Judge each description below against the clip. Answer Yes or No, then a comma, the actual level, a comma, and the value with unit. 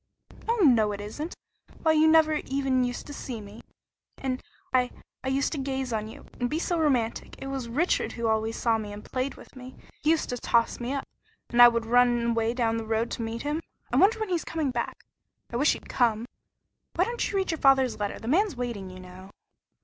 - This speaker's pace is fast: Yes, fast, 225 wpm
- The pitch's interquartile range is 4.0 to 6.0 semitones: Yes, average, 4.5 semitones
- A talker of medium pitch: No, very high, 250 Hz